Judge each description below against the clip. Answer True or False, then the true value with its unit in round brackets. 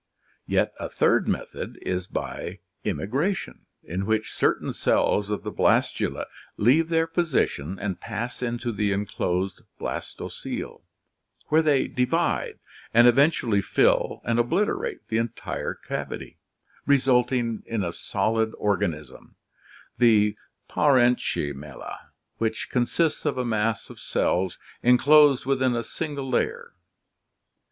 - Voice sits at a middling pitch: False (120 Hz)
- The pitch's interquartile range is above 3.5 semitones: True (5.1 semitones)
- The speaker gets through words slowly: True (115 wpm)